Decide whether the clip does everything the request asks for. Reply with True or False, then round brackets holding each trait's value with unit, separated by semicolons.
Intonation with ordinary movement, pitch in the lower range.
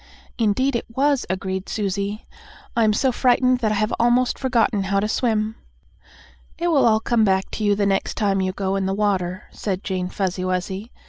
False (3.5 semitones; 210 Hz)